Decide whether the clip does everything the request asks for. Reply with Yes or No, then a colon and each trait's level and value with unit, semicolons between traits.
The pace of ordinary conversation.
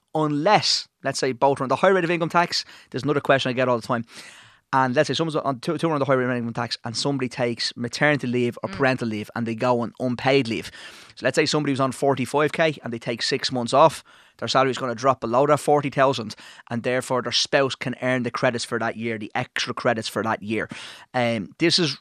No: fast, 250 wpm